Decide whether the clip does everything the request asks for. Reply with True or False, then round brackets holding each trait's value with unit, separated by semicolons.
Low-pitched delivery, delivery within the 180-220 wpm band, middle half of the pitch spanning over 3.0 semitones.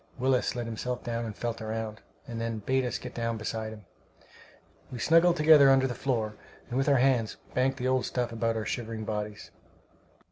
False (120 Hz; 190 wpm; 2.7 semitones)